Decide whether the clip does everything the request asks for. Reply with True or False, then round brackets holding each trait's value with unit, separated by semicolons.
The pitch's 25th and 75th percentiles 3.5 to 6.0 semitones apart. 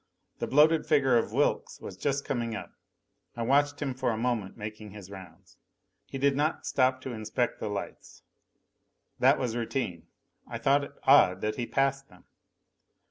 True (4.4 semitones)